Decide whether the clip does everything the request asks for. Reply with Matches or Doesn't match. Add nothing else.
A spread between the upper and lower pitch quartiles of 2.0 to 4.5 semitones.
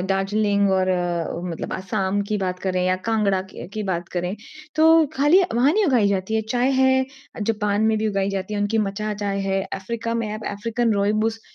Matches